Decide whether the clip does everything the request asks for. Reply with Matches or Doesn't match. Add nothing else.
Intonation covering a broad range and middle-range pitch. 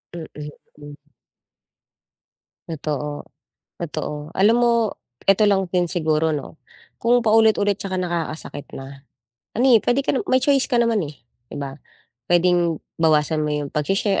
Matches